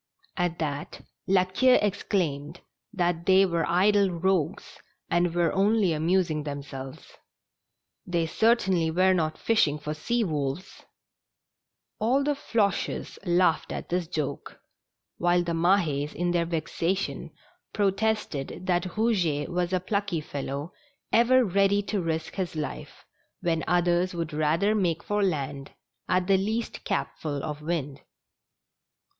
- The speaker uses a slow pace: Yes, slow, 130 wpm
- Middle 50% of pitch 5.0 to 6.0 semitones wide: No, average, 3.8 semitones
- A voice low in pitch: No, medium, 175 Hz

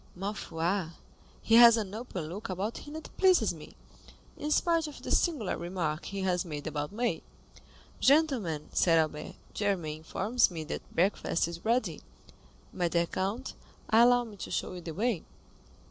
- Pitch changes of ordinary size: No, wide, 6.0 semitones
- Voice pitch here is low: No, high, 195 Hz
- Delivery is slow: No, average, 160 wpm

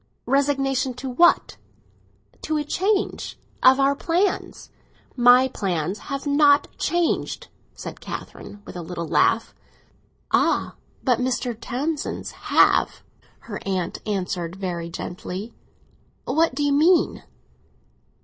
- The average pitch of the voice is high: Yes, very high, 255 Hz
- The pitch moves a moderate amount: No, wide, 6.6 semitones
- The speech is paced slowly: Yes, slow, 110 wpm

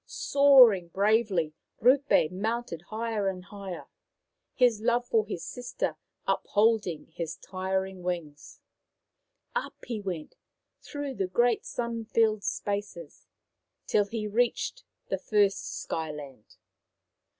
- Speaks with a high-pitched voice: Yes, high, 210 Hz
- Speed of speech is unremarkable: No, slow, 110 wpm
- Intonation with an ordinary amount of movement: Yes, average, 4.3 semitones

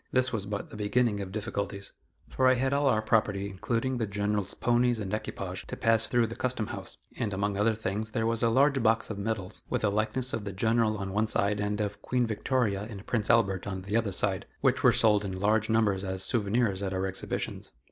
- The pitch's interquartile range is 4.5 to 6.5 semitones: No, narrow, 2.4 semitones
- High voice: No, low, 110 Hz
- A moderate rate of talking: No, fast, 225 wpm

